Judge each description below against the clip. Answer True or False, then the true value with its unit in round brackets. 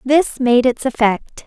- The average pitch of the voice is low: False (250 Hz)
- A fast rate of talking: False (165 wpm)